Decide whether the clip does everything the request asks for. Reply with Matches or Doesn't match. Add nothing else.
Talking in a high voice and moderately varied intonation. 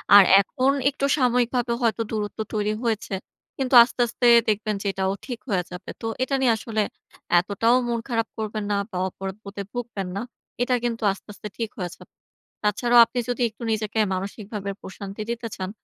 Matches